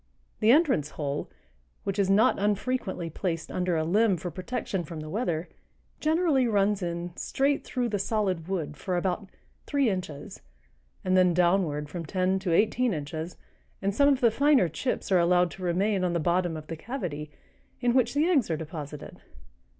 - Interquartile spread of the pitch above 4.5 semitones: Yes, average, 5.1 semitones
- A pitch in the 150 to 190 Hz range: Yes, medium, 185 Hz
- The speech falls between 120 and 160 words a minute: No, average, 175 wpm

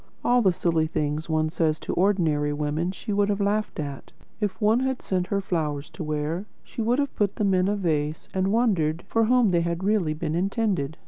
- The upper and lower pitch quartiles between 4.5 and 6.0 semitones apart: Yes, average, 4.8 semitones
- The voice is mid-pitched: Yes, medium, 180 Hz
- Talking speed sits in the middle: No, fast, 210 wpm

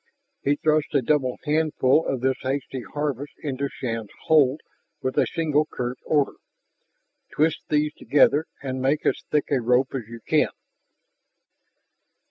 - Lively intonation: No, average, 2.7 semitones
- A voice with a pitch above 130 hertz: Yes, medium, 140 Hz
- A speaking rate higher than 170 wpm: No, average, 140 wpm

